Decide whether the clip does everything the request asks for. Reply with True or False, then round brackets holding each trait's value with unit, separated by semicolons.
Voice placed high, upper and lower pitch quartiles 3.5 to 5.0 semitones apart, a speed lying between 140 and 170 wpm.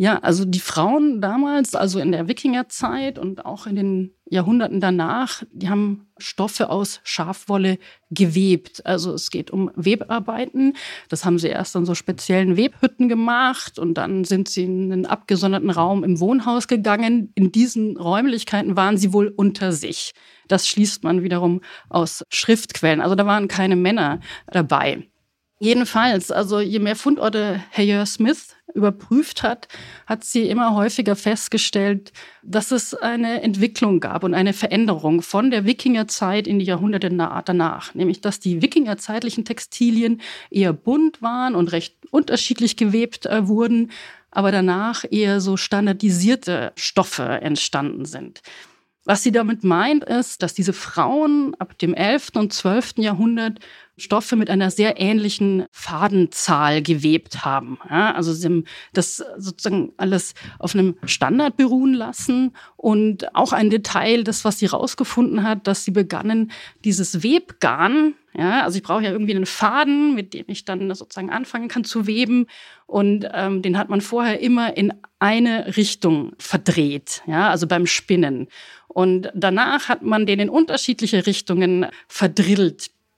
True (205 Hz; 3.8 semitones; 150 wpm)